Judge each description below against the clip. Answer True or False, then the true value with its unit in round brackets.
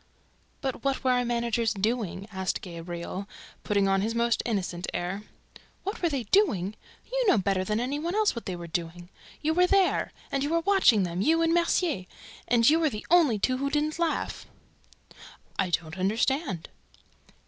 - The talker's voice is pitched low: False (235 Hz)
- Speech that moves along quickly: False (175 wpm)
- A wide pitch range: True (8.4 semitones)